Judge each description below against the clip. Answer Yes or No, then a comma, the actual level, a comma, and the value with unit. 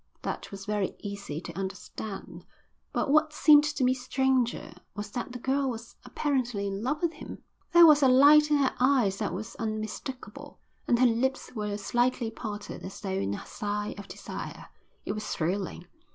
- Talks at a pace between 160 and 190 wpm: Yes, average, 180 wpm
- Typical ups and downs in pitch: Yes, average, 4.7 semitones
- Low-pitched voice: No, high, 235 Hz